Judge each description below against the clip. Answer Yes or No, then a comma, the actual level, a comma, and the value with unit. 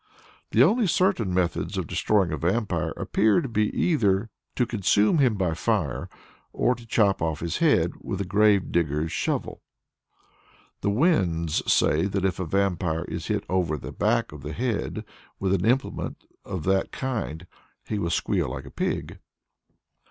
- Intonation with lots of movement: No, average, 4.9 semitones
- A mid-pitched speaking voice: No, very low, 95 Hz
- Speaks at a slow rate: No, average, 165 wpm